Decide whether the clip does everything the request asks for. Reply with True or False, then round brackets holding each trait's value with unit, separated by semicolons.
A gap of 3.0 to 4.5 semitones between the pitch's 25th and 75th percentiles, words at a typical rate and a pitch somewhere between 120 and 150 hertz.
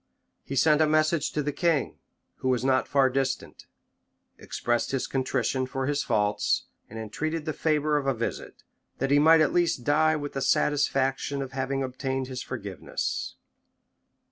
False (2.5 semitones; 165 wpm; 135 Hz)